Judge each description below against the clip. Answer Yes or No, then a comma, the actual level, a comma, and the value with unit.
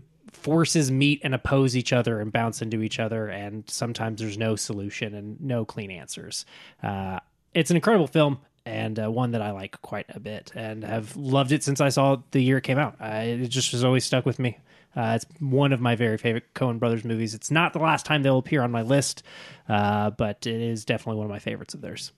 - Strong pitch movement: No, average, 3.9 semitones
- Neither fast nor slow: No, fast, 230 wpm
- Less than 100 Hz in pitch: No, low, 120 Hz